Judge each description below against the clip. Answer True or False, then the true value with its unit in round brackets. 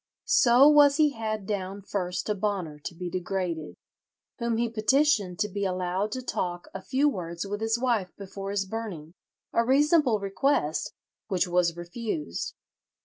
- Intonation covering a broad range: False (4.6 semitones)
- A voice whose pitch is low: False (200 Hz)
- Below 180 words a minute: True (150 wpm)